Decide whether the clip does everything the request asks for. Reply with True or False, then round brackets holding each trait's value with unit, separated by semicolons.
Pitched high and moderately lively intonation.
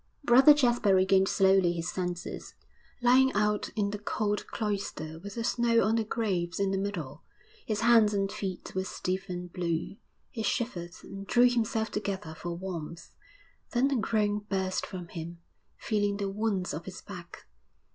True (200 Hz; 3.5 semitones)